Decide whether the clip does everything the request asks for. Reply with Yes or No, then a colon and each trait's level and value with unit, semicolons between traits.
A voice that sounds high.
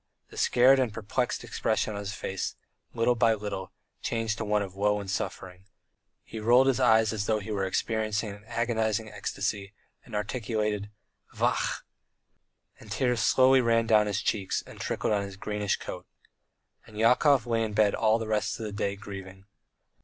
No: low, 110 Hz